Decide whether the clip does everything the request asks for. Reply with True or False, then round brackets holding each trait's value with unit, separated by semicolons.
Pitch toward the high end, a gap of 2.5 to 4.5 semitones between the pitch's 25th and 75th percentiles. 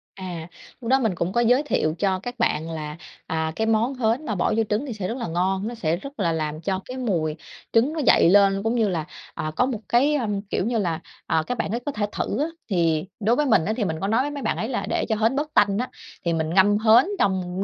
False (205 Hz; 5.5 semitones)